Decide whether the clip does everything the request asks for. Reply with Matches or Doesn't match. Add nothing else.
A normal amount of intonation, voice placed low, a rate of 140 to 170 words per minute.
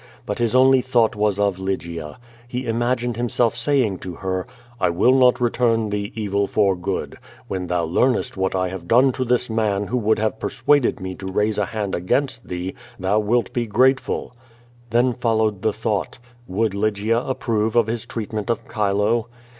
Doesn't match